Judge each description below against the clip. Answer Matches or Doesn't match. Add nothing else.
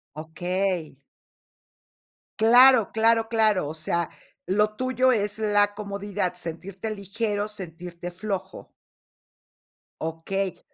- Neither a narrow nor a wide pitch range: Matches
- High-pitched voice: Matches